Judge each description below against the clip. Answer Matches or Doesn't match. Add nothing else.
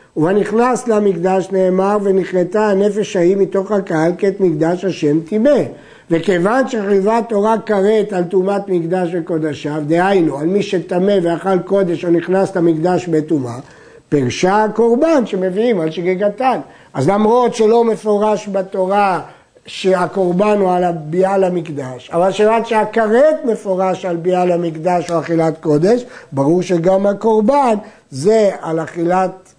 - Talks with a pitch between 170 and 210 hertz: Matches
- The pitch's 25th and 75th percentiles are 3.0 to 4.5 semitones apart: Matches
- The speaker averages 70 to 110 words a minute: Doesn't match